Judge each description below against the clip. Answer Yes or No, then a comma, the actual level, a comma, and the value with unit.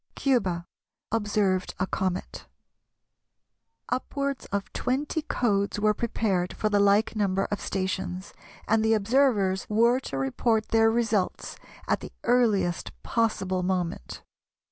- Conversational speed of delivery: No, slow, 120 wpm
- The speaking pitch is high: Yes, high, 205 Hz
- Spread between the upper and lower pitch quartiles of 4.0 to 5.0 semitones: No, average, 3.4 semitones